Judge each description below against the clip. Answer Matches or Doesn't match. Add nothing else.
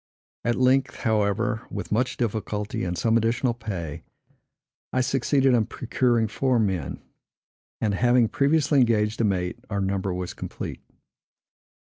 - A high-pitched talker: Doesn't match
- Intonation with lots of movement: Doesn't match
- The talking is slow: Matches